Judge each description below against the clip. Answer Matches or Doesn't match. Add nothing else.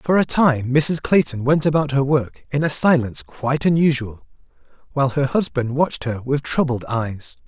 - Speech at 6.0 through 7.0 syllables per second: Doesn't match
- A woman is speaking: Doesn't match